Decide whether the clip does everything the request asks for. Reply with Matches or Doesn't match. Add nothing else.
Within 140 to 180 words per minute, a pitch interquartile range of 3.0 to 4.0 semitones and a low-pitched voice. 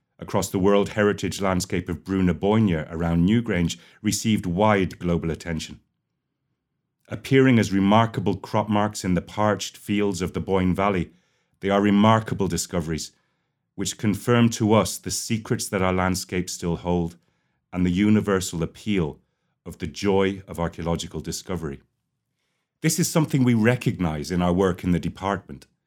Matches